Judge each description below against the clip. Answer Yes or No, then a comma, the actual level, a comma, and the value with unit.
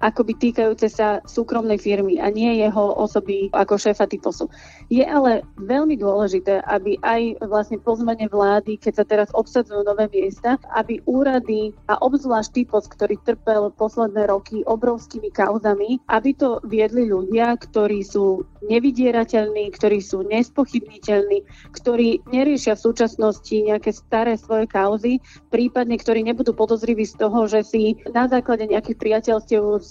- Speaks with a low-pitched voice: No, high, 220 Hz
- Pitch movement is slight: Yes, narrow, 2.1 semitones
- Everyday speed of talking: Yes, average, 135 wpm